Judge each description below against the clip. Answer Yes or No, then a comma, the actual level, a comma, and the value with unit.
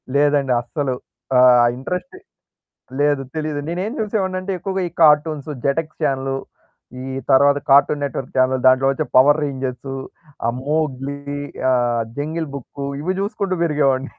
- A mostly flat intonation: No, average, 3.1 semitones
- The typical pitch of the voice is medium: Yes, medium, 145 Hz